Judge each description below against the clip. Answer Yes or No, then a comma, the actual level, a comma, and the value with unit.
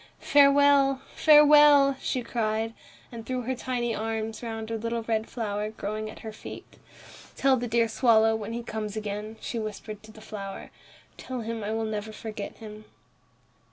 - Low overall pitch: No, high, 225 Hz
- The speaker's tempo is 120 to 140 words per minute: No, average, 165 wpm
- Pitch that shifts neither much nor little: No, narrow, 2.2 semitones